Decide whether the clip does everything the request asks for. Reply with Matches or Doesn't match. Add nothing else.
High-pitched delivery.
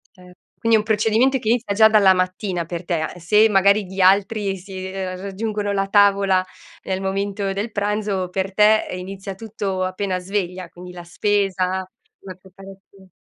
Matches